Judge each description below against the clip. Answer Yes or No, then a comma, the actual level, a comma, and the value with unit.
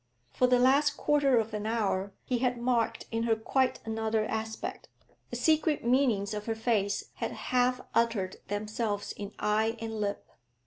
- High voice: Yes, high, 225 Hz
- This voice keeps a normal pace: Yes, average, 165 wpm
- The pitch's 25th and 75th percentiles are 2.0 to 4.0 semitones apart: Yes, average, 2.9 semitones